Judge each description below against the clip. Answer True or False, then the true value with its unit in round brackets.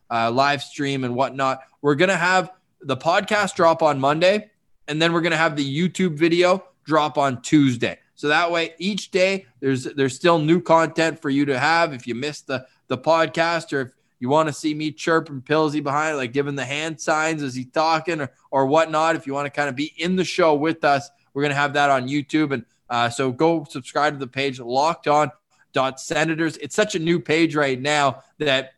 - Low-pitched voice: False (150 Hz)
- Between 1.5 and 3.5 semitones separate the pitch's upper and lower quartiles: True (3.1 semitones)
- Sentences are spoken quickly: True (215 wpm)